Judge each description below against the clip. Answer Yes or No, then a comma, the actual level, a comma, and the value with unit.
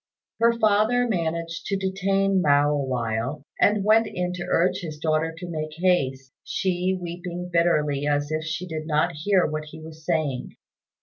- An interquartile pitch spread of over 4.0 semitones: No, average, 3.6 semitones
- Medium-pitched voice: Yes, medium, 170 Hz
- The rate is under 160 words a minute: No, average, 165 wpm